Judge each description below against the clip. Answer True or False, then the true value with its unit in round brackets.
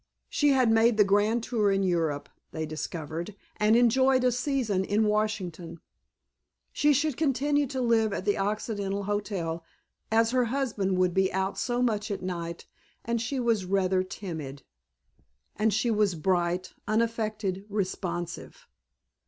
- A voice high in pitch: True (210 Hz)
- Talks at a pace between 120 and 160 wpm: True (145 wpm)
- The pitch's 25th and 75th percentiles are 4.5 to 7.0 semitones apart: False (4.0 semitones)